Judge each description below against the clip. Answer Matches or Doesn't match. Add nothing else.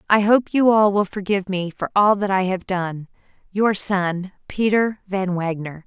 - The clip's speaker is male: Doesn't match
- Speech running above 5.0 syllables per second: Doesn't match